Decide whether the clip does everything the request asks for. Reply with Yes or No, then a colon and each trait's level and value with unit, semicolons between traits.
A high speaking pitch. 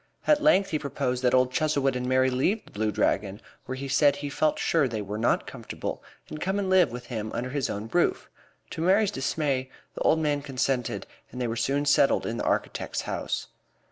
No: low, 135 Hz